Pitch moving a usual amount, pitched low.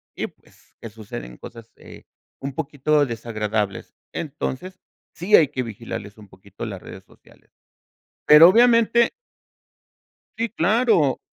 No: wide, 8.4 semitones; low, 130 Hz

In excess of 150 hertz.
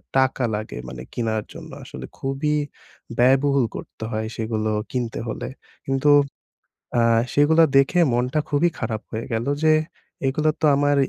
No: low, 130 Hz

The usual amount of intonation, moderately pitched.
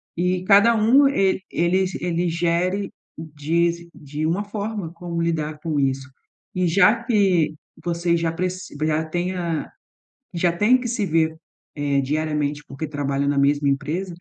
Yes: average, 3.6 semitones; medium, 170 Hz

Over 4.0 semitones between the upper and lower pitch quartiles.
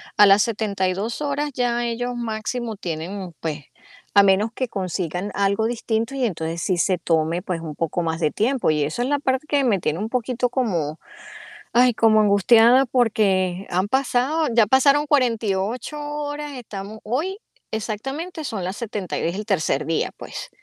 Yes: average, 5.2 semitones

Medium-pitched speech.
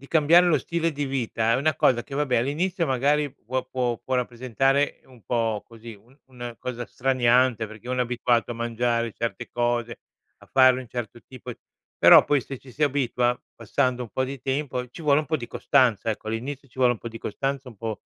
No: low, 125 Hz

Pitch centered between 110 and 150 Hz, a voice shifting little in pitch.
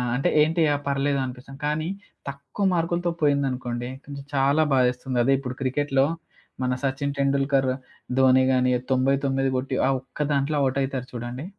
Yes: low, 135 Hz; narrow, 1.5 semitones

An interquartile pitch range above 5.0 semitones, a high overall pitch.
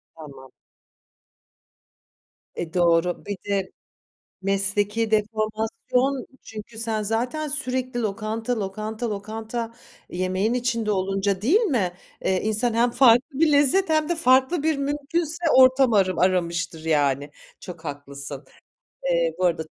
Yes: wide, 5.6 semitones; high, 220 Hz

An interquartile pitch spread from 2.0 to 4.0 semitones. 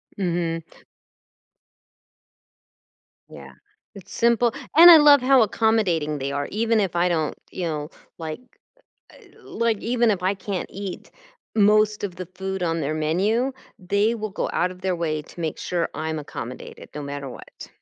No: wide, 5.4 semitones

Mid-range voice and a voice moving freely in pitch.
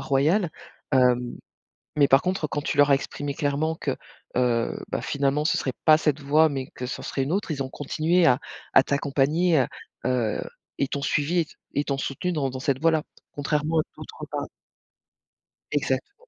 No: medium, 145 Hz; average, 2.8 semitones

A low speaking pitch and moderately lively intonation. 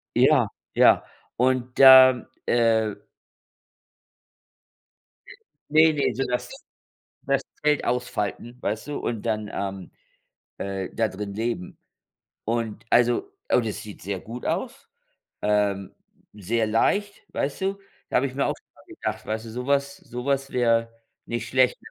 Yes: low, 115 Hz; average, 3.4 semitones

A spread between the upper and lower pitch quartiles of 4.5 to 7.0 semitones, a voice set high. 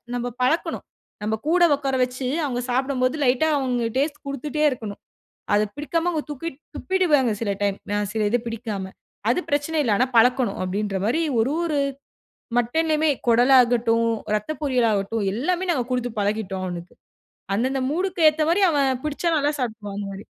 Yes: average, 5.1 semitones; very high, 250 Hz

